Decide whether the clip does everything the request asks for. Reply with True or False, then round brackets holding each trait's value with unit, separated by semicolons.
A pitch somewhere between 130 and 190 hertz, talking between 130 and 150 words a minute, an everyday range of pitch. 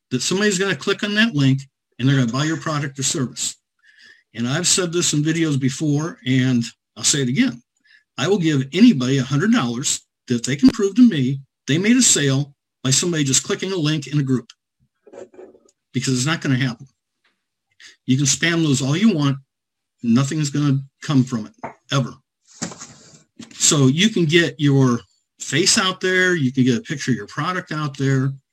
False (140 Hz; 185 wpm; 4.9 semitones)